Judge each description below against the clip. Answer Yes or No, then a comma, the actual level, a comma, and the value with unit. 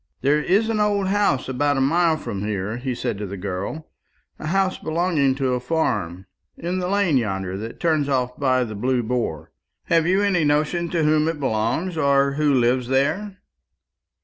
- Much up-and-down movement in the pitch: Yes, wide, 5.7 semitones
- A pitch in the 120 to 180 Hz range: Yes, medium, 140 Hz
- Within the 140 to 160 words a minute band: No, average, 185 wpm